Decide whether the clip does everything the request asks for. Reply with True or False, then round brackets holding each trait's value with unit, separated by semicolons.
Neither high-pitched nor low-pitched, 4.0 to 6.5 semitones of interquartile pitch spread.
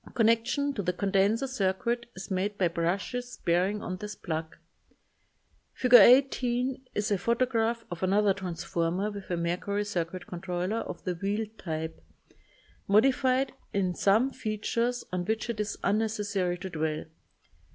False (205 Hz; 4.3 semitones)